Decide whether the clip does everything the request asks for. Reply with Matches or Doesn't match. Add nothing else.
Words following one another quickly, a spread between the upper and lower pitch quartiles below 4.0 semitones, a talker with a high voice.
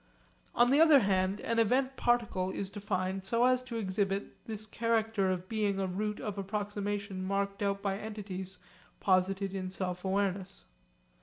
Doesn't match